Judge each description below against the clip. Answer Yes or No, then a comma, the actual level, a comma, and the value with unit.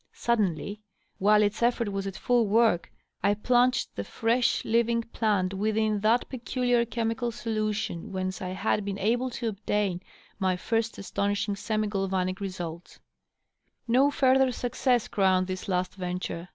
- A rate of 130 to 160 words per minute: Yes, average, 140 wpm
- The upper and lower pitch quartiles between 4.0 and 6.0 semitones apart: No, average, 3.6 semitones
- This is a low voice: No, high, 210 Hz